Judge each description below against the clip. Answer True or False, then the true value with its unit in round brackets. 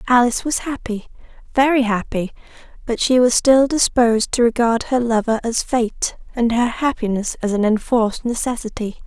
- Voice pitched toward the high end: True (235 Hz)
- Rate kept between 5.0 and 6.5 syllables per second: True (5.1 syllables/s)